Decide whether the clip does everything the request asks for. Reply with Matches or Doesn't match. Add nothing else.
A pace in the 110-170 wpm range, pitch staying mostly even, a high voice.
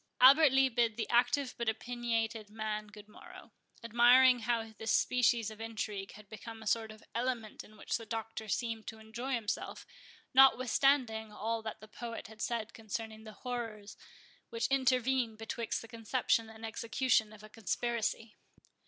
Matches